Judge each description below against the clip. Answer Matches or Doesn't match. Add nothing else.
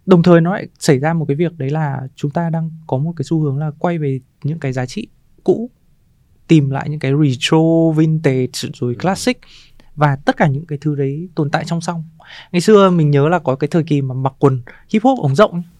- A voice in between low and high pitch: Matches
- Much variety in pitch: Doesn't match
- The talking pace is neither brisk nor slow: Matches